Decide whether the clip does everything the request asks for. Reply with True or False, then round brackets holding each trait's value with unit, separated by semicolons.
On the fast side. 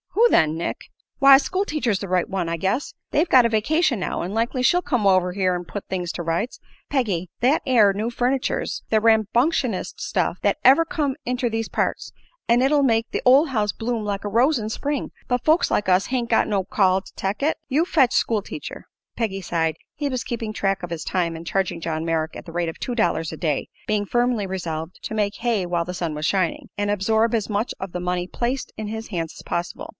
True (225 wpm)